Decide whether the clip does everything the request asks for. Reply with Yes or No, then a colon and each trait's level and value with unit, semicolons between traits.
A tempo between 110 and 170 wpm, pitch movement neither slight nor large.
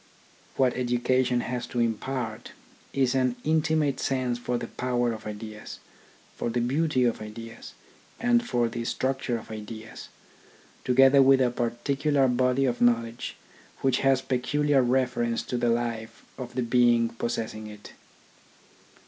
No: average, 140 wpm; narrow, 2.2 semitones